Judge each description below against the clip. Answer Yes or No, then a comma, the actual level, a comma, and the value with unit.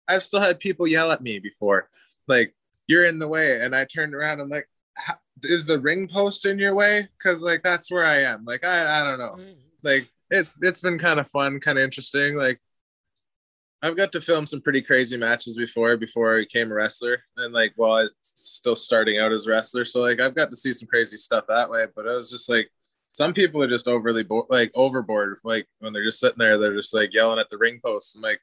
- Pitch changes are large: Yes, wide, 7.0 semitones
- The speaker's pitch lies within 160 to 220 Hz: No, low, 135 Hz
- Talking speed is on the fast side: Yes, fast, 240 wpm